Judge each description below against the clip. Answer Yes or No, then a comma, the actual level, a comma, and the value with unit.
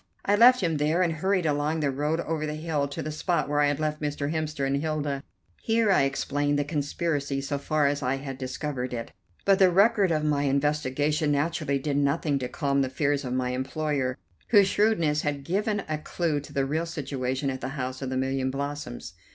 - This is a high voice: No, medium, 145 Hz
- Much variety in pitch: No, narrow, 2.5 semitones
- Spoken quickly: Yes, fast, 210 wpm